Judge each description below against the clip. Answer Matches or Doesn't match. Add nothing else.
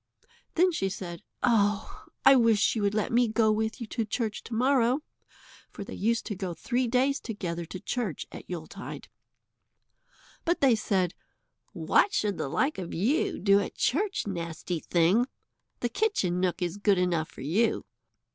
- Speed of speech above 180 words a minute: Doesn't match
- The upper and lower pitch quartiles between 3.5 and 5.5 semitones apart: Matches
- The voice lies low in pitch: Doesn't match